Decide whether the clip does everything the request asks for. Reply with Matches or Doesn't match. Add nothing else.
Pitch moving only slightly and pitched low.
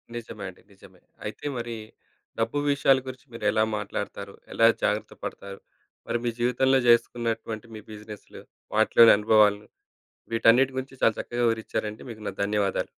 Matches